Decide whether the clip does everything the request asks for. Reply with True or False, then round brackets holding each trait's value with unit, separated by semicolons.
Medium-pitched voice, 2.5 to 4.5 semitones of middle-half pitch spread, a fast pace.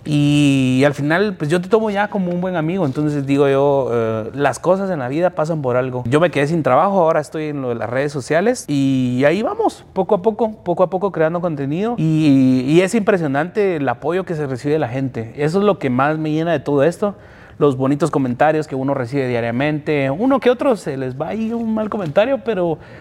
False (155 Hz; 5.2 semitones; 230 wpm)